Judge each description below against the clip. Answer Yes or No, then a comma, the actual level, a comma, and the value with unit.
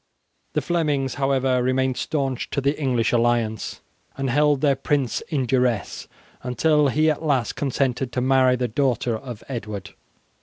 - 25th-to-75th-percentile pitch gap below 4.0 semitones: Yes, narrow, 2.4 semitones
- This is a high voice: No, low, 130 Hz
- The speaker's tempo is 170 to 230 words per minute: No, average, 150 wpm